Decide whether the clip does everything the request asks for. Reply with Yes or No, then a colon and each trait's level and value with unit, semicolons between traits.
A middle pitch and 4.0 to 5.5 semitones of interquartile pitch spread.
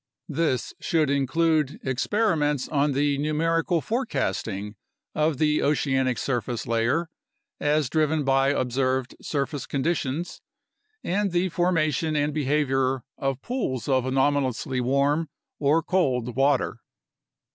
No: medium, 145 Hz; average, 3.2 semitones